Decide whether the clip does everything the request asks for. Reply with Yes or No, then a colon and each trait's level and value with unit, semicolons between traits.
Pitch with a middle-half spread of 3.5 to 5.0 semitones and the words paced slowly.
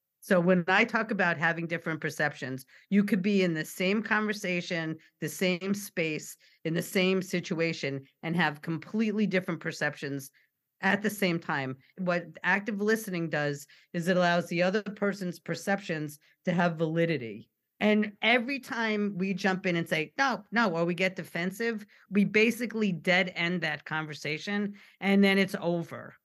No: average, 3.8 semitones; average, 160 wpm